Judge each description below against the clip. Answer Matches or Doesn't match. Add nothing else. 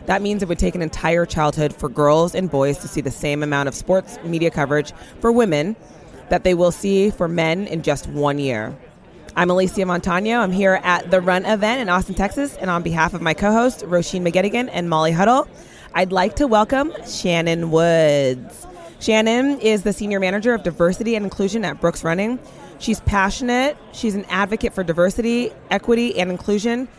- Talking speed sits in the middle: Matches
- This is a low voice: Doesn't match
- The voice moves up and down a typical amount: Matches